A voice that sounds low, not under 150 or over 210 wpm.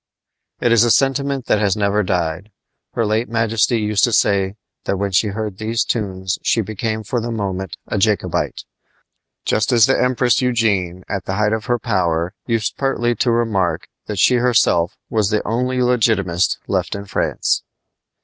Yes: low, 110 Hz; average, 170 wpm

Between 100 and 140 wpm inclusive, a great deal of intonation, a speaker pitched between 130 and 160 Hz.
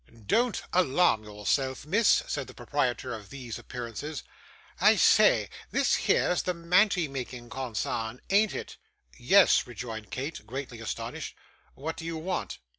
Yes: slow, 135 wpm; wide, 6.1 semitones; low, 135 Hz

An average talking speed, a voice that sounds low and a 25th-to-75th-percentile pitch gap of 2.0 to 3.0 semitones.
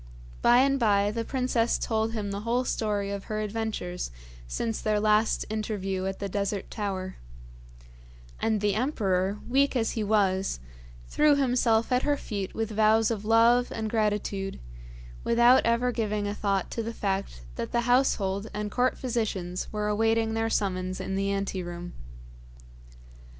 No: average, 155 wpm; high, 215 Hz; narrow, 2.6 semitones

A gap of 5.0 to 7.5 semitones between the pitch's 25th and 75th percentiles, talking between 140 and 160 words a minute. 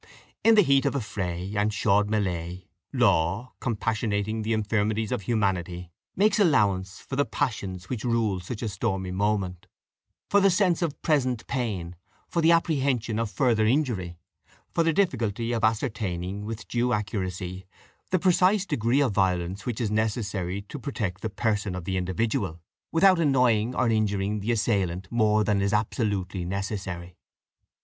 No: average, 4.4 semitones; average, 155 wpm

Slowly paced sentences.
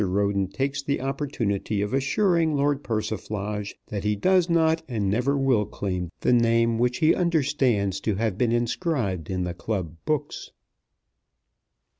No: average, 145 wpm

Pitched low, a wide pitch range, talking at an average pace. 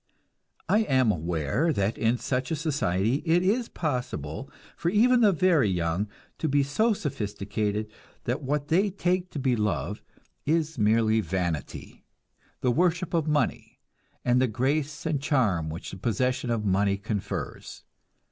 Yes: low, 130 Hz; wide, 7.6 semitones; average, 145 wpm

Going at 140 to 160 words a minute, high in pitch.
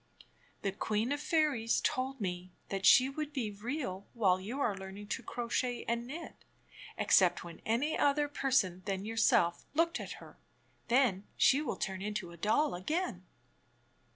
Yes: average, 155 wpm; high, 230 Hz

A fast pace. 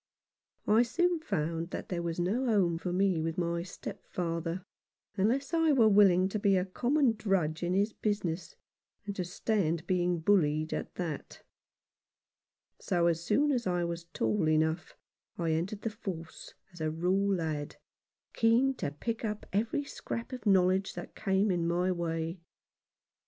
No: average, 155 wpm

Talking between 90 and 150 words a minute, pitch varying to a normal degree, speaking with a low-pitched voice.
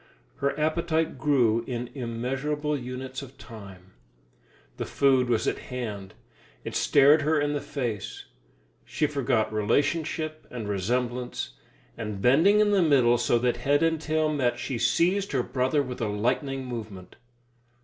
Yes: average, 145 wpm; average, 4.1 semitones; low, 130 Hz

